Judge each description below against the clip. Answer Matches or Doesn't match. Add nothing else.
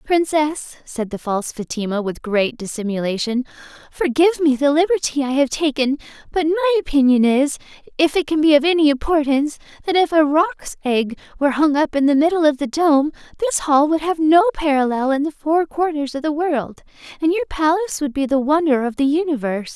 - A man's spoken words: Doesn't match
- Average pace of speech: Matches